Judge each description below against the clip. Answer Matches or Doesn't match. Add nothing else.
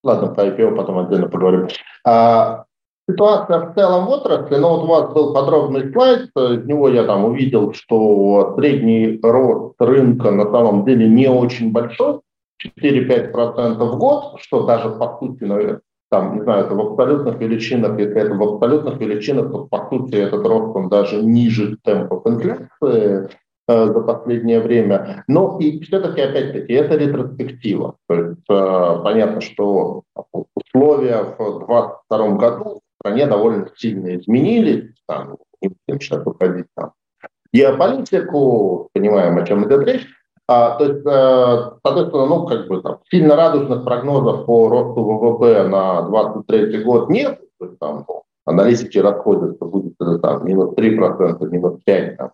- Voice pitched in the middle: Doesn't match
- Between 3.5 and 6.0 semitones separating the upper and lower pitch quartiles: Matches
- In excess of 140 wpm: Matches